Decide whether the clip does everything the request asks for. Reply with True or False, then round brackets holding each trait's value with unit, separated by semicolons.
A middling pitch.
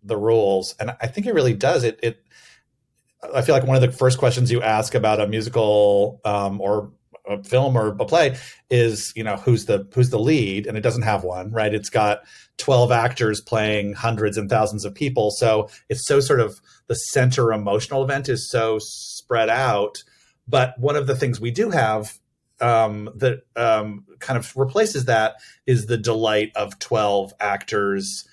False (115 Hz)